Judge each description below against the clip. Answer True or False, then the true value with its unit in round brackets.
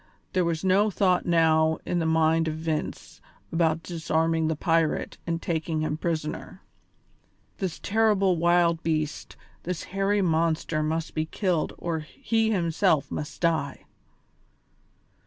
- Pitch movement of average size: False (2.2 semitones)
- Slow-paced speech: True (130 wpm)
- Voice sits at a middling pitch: True (165 Hz)